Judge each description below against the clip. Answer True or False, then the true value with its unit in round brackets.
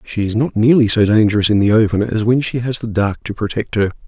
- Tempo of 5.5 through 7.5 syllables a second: True (6.0 syllables/s)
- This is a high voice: False (110 Hz)